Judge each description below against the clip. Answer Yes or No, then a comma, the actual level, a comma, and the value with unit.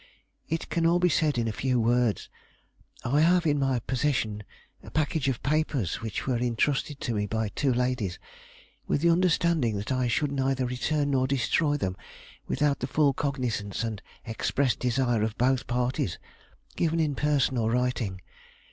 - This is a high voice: No, low, 130 Hz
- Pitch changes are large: No, average, 4.0 semitones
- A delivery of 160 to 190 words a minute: Yes, average, 165 wpm